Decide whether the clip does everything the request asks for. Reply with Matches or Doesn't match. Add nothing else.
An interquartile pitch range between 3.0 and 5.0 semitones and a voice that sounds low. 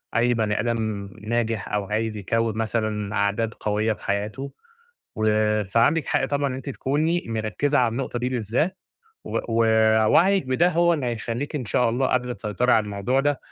Matches